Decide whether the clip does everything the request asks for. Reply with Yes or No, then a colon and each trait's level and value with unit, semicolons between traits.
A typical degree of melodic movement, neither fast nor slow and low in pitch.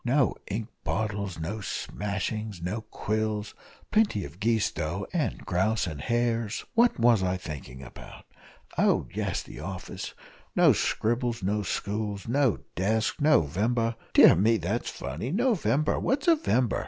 Yes: average, 3.9 semitones; average, 145 wpm; low, 110 Hz